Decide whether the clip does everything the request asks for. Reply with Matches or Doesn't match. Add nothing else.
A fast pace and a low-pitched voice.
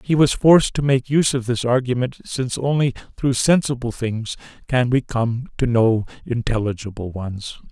Doesn't match